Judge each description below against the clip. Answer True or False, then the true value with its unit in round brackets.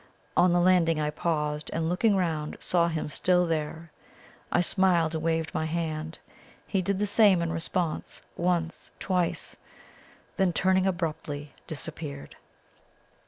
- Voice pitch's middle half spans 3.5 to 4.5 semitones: False (2.4 semitones)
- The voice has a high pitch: False (170 Hz)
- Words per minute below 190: True (135 wpm)